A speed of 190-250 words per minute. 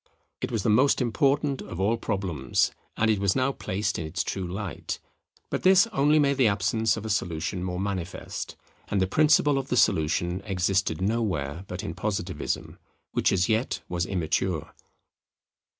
No: average, 165 wpm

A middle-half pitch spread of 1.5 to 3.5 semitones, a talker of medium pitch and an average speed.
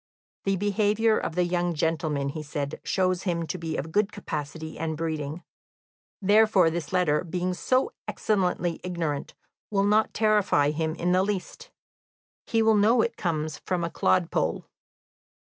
No: average, 4.3 semitones; medium, 180 Hz; average, 150 wpm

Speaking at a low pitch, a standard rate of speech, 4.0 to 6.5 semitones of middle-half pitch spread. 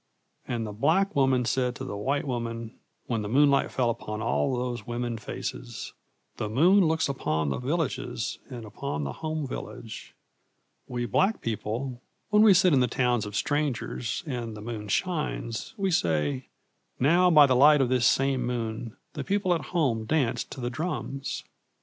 Yes: low, 125 Hz; average, 170 wpm; average, 4.7 semitones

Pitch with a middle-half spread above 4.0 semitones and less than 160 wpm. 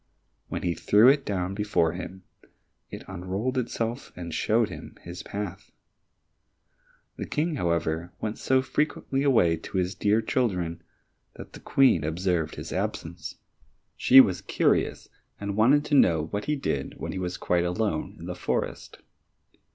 Yes: wide, 5.5 semitones; average, 150 wpm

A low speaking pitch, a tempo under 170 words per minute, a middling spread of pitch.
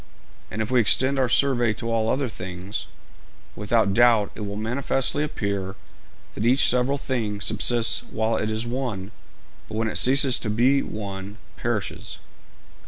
Yes: low, 115 Hz; average, 155 wpm; average, 3.3 semitones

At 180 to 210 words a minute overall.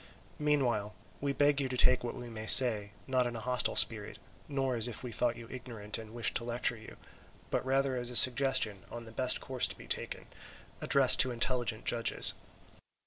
Yes: average, 195 wpm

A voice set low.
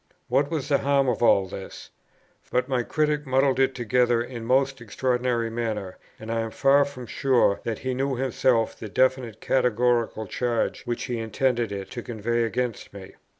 Yes: low, 125 Hz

